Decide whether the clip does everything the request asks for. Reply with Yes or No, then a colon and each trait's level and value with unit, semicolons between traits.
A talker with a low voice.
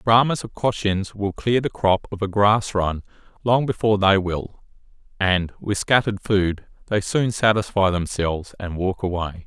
Yes: low, 100 Hz